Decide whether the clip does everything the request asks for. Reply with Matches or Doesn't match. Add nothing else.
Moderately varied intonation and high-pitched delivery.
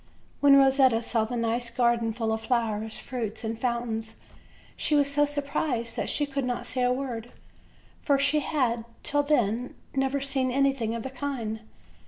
Matches